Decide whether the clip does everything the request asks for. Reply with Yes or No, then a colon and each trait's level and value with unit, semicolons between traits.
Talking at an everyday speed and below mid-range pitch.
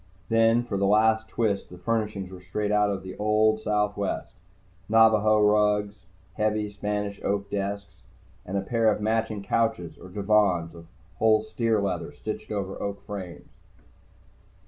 Yes: average, 145 wpm; low, 105 Hz